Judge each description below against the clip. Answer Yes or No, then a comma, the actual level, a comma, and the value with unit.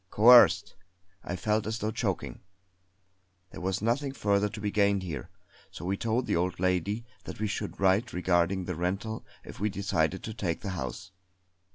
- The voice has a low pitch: Yes, low, 100 Hz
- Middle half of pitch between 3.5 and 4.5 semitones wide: No, average, 2.9 semitones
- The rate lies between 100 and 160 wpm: No, average, 175 wpm